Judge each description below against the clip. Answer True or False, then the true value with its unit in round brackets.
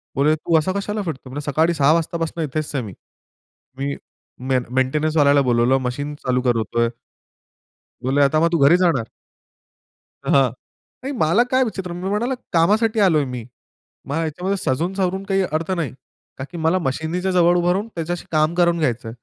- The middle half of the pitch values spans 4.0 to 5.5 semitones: True (4.6 semitones)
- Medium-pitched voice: True (160 Hz)